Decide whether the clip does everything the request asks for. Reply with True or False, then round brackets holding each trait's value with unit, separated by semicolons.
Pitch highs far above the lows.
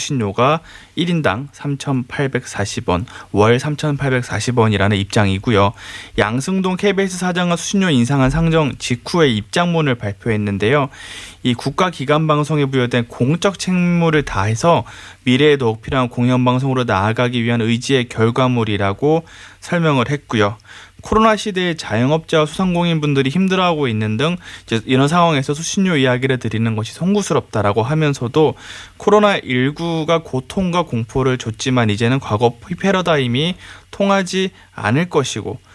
True (6.1 semitones)